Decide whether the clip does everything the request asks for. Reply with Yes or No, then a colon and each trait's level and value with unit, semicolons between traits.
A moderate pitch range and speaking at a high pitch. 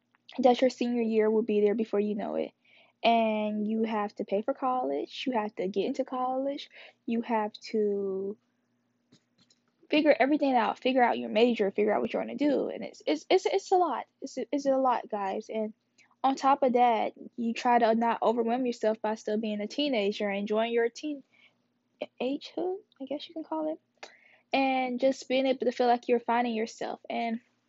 Yes: average, 3.5 semitones; high, 240 Hz